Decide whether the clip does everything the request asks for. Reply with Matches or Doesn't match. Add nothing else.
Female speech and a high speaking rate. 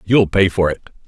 Doesn't match